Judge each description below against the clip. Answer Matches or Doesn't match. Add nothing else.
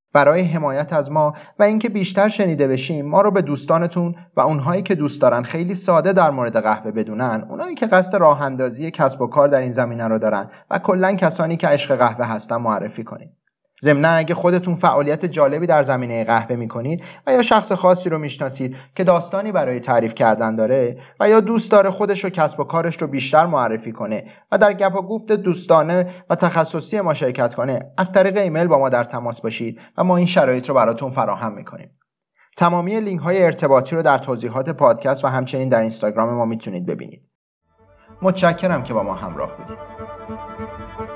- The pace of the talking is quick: Matches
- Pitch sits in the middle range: Matches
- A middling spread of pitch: Doesn't match